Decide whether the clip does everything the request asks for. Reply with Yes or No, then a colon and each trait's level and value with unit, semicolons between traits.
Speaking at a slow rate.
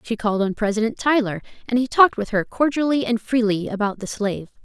No: fast, 205 wpm